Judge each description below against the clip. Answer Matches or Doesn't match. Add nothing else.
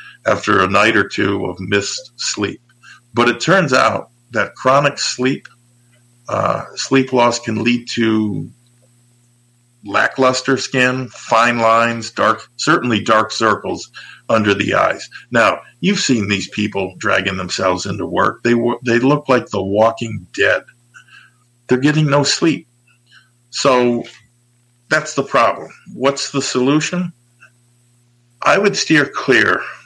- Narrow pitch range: Matches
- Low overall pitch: Matches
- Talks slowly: Matches